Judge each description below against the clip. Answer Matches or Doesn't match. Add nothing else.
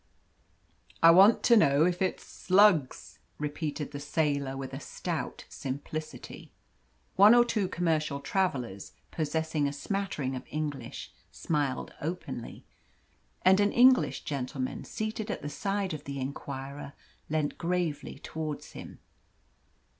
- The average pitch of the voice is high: Doesn't match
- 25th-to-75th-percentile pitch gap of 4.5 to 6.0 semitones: Matches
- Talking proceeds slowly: Matches